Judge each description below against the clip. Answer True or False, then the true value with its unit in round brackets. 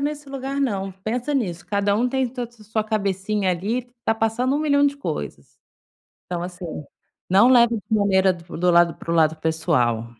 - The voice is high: True (210 Hz)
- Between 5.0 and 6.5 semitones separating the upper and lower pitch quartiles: True (5.6 semitones)